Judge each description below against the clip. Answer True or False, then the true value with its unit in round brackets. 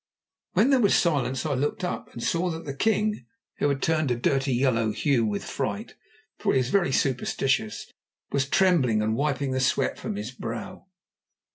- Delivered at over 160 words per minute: True (180 wpm)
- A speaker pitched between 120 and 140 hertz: True (135 Hz)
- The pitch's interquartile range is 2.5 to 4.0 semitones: False (4.9 semitones)